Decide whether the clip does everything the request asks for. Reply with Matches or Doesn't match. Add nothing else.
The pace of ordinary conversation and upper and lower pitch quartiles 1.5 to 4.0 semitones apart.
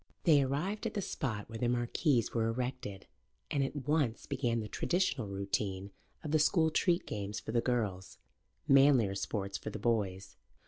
Doesn't match